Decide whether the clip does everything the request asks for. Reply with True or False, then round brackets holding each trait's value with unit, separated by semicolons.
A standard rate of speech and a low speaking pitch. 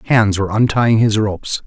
True (180 wpm; 105 Hz)